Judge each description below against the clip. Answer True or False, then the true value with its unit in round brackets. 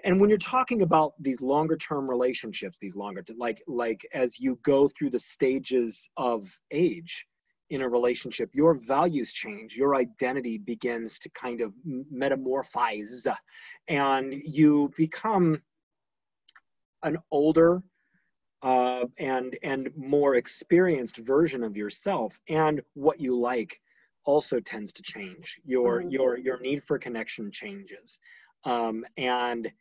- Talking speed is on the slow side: True (130 wpm)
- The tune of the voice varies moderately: True (4.1 semitones)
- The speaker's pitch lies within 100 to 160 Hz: True (135 Hz)